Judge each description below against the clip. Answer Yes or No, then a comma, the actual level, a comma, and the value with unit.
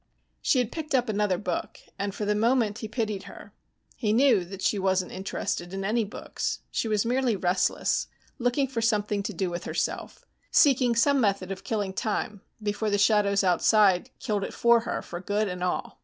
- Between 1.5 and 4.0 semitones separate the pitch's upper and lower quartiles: Yes, average, 3.2 semitones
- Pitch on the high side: Yes, high, 210 Hz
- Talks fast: No, average, 190 wpm